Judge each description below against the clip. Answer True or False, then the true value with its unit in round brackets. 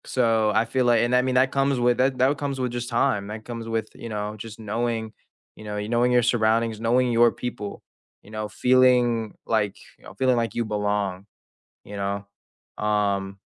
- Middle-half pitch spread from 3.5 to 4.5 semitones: False (2.7 semitones)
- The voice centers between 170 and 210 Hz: False (115 Hz)